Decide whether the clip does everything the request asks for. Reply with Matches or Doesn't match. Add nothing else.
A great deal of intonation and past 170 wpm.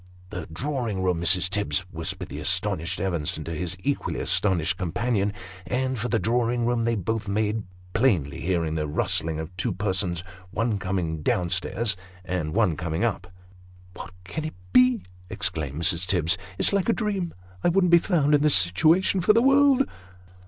Matches